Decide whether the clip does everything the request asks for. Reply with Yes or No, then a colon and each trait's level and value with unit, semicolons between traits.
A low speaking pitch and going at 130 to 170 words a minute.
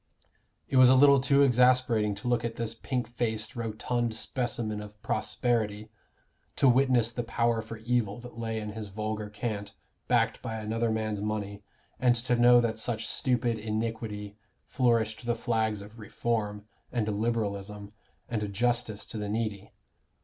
Yes: low, 115 Hz; average, 155 wpm